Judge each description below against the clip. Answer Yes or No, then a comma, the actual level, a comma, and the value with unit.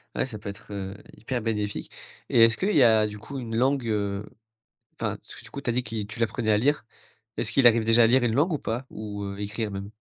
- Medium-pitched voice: No, low, 115 Hz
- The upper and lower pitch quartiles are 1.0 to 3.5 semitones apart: Yes, average, 3.0 semitones